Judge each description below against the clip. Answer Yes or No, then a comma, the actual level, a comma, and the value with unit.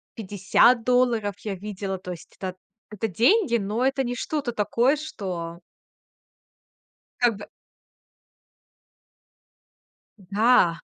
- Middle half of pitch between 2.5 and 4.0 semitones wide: No, average, 4.4 semitones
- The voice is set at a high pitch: Yes, high, 210 Hz